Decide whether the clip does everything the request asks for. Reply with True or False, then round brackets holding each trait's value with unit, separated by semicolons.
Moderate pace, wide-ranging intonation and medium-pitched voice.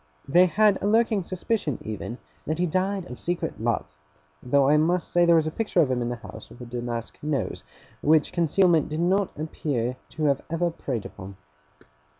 True (190 wpm; 6.2 semitones; 155 Hz)